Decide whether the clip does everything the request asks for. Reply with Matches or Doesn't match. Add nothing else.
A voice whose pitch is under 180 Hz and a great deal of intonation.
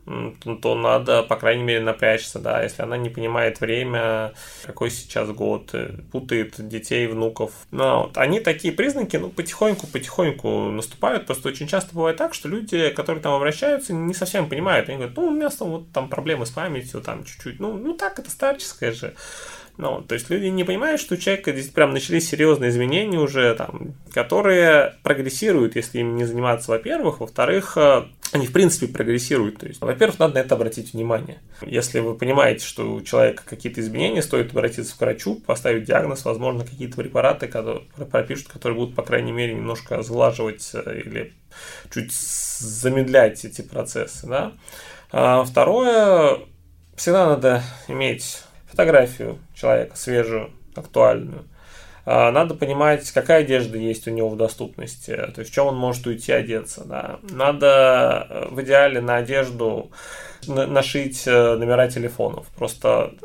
Matches